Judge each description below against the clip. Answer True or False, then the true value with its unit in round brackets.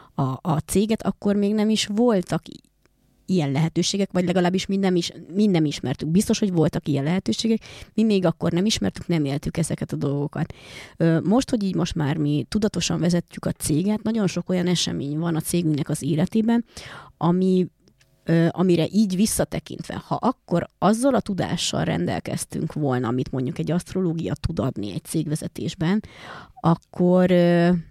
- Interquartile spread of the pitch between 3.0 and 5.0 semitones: True (3.6 semitones)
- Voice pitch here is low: False (175 Hz)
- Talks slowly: False (150 wpm)